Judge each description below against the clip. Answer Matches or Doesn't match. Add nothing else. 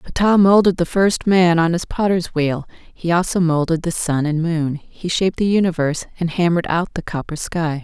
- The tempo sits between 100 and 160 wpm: Doesn't match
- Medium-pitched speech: Matches